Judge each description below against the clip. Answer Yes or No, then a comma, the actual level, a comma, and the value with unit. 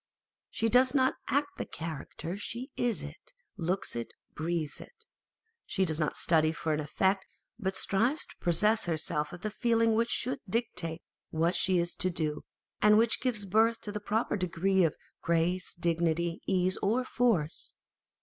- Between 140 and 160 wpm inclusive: No, average, 170 wpm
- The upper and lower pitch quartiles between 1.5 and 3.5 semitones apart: No, average, 5.3 semitones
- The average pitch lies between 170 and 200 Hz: Yes, high, 190 Hz